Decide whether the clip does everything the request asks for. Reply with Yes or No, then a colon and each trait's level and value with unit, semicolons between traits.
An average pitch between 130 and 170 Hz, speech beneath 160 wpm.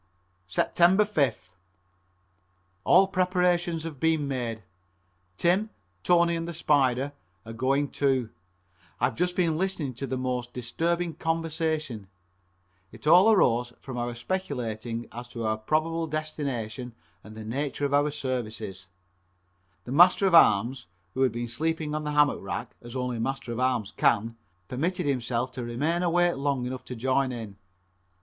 Yes: low, 135 Hz; average, 150 wpm